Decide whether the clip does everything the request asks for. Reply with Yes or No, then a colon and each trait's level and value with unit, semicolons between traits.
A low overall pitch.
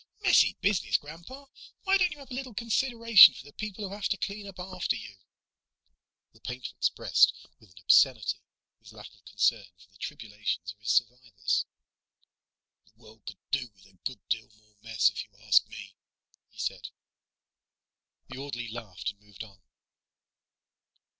Yes: low, 125 Hz